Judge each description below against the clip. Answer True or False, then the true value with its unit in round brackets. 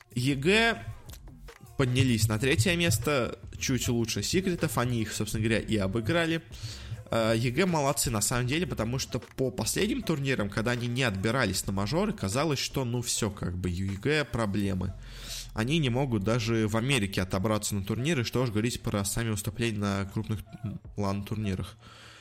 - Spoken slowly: False (150 wpm)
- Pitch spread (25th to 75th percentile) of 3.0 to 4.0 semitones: True (3.7 semitones)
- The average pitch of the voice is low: True (115 Hz)